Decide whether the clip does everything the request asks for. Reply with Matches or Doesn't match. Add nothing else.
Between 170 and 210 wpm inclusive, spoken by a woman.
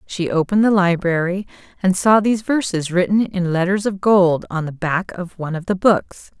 Matches